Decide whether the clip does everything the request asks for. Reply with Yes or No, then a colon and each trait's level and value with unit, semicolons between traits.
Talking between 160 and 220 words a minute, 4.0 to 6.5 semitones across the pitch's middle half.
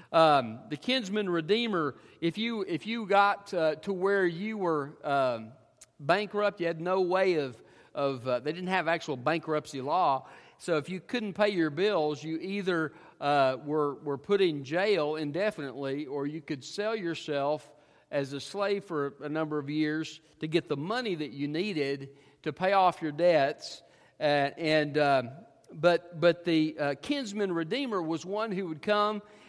Yes: average, 170 wpm; average, 4.8 semitones